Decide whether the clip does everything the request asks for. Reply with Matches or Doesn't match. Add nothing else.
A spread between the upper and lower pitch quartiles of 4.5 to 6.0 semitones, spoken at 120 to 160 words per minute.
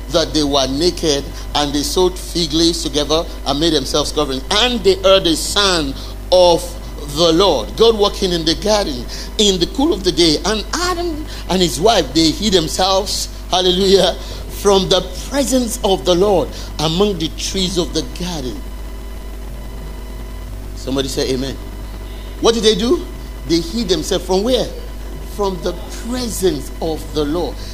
Matches